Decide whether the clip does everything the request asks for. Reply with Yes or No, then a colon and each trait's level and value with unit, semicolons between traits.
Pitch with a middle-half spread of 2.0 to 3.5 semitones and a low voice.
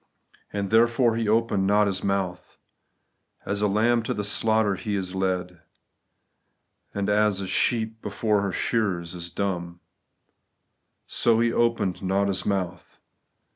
Yes: average, 2.8 semitones; low, 100 Hz